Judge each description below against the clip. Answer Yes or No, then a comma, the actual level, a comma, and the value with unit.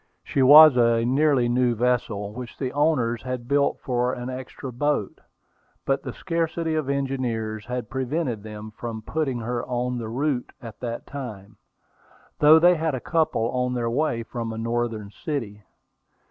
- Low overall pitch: Yes, low, 125 Hz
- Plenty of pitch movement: No, average, 3.4 semitones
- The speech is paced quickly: No, average, 160 wpm